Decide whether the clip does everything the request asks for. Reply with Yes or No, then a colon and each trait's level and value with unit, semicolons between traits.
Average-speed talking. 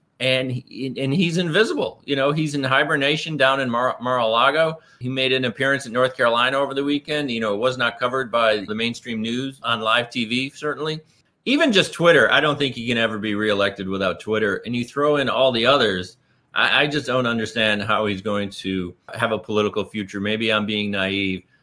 No: fast, 210 wpm